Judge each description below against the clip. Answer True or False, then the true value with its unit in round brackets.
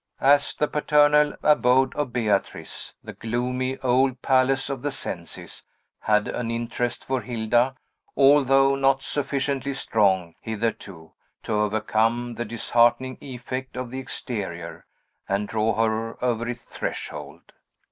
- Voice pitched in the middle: False (120 Hz)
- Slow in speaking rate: True (125 wpm)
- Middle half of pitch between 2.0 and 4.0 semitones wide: True (3.3 semitones)